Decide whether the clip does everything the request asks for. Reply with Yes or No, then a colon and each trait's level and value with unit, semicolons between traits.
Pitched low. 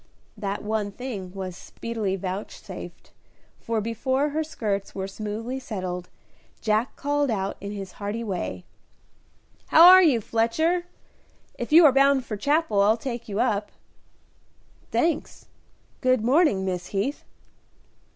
No: high, 220 Hz